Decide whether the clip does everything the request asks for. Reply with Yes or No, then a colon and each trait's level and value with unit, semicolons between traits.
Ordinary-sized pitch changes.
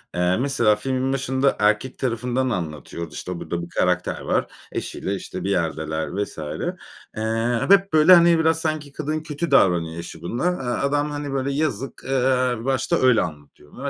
No: wide, 7.5 semitones